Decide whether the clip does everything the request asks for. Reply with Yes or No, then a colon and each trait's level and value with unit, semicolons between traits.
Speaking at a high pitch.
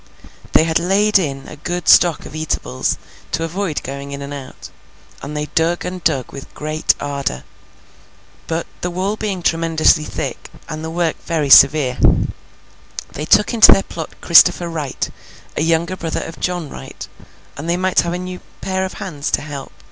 No: medium, 165 Hz